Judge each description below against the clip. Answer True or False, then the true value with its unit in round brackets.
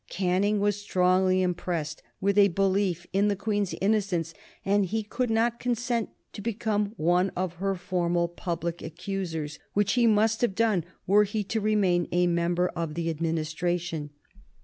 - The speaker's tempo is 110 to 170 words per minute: True (155 wpm)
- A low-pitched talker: False (190 Hz)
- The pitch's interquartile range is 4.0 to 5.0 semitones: False (3.2 semitones)